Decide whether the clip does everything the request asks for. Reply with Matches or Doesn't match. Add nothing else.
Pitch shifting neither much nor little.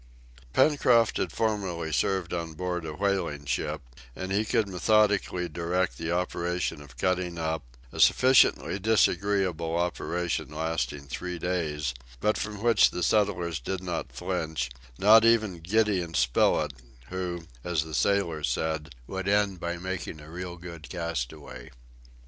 Matches